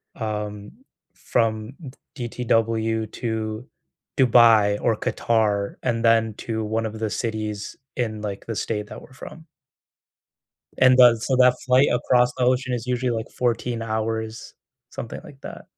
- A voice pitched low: Yes, low, 115 Hz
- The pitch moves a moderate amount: No, narrow, 2.1 semitones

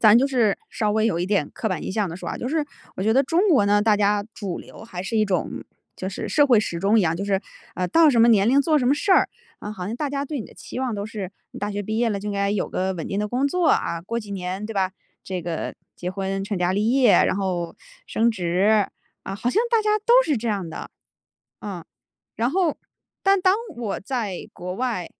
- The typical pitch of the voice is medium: No, high, 210 Hz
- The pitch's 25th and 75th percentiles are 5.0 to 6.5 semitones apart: No, average, 4.6 semitones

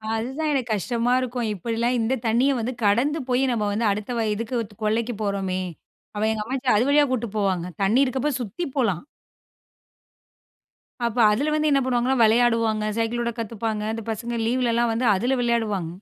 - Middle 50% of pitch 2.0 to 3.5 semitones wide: Yes, average, 2.8 semitones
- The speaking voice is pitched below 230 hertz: No, high, 235 Hz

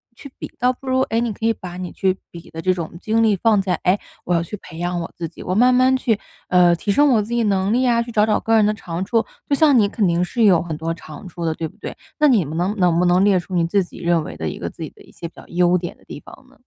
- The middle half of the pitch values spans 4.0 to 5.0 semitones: Yes, average, 4.7 semitones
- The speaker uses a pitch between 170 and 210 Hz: Yes, high, 190 Hz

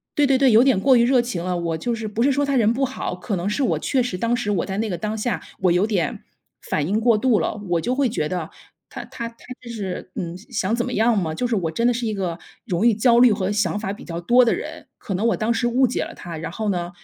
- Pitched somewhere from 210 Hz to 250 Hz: Yes, high, 220 Hz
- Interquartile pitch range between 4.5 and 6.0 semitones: Yes, average, 4.8 semitones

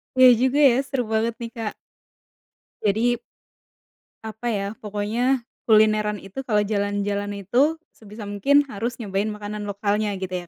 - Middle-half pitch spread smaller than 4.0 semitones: Yes, narrow, 2.6 semitones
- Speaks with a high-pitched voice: Yes, high, 210 Hz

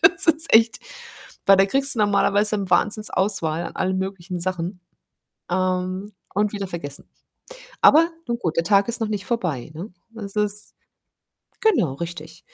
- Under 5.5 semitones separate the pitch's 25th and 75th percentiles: Yes, average, 2.9 semitones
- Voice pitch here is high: Yes, high, 195 Hz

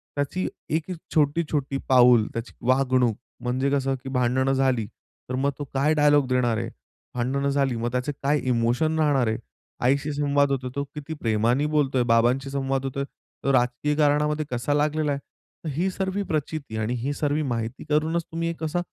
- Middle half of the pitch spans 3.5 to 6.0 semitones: No, average, 2.9 semitones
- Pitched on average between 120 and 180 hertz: Yes, medium, 140 Hz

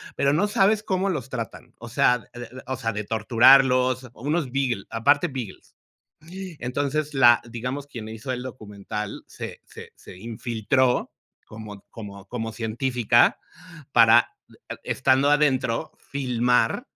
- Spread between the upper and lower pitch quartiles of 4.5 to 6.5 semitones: No, average, 3.4 semitones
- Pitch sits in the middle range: No, low, 125 Hz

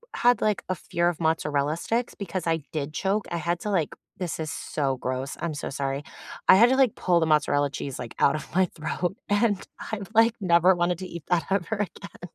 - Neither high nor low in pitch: Yes, medium, 170 Hz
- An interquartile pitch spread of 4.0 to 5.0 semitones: Yes, average, 4.5 semitones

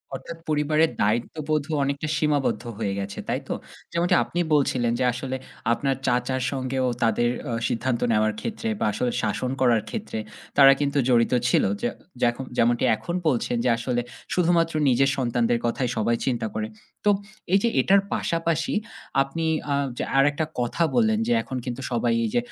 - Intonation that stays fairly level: No, average, 4.5 semitones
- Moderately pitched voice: No, low, 130 Hz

